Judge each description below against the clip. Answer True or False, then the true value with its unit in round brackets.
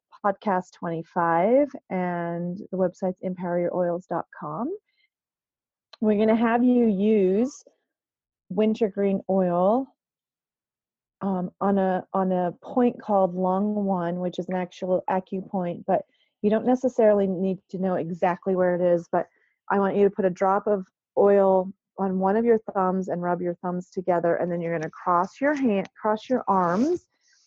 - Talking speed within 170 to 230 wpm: False (155 wpm)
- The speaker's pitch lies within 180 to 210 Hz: True (190 Hz)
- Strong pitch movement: False (3.2 semitones)